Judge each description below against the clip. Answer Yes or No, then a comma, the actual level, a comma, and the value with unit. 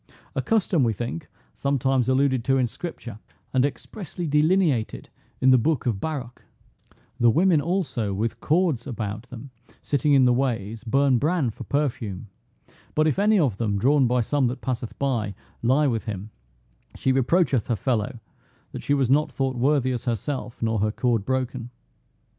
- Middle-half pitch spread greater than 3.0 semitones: Yes, average, 3.8 semitones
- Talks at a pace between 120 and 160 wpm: No, average, 170 wpm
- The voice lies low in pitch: Yes, low, 130 Hz